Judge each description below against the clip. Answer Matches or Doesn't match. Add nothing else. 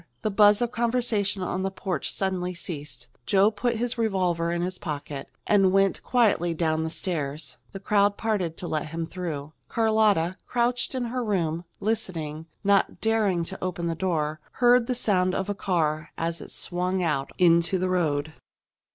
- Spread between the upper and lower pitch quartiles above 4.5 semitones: Doesn't match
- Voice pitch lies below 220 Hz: Matches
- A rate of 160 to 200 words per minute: Matches